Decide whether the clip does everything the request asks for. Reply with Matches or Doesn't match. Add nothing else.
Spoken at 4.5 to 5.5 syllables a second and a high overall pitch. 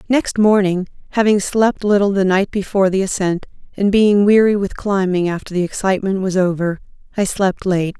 Matches